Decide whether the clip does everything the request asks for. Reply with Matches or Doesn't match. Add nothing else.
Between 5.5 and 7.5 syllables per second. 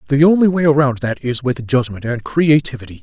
Matches